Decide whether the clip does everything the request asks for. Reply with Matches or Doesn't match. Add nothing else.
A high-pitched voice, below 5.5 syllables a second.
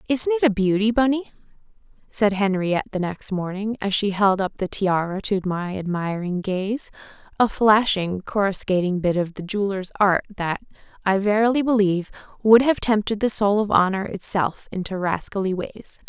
Matches